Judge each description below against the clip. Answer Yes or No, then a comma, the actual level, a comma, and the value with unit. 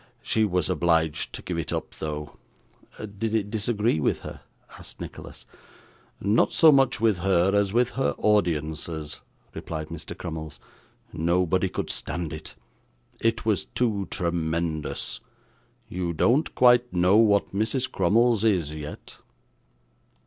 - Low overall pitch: Yes, very low, 90 Hz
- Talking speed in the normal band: No, slow, 130 wpm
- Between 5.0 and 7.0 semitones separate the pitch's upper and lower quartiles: Yes, wide, 5.4 semitones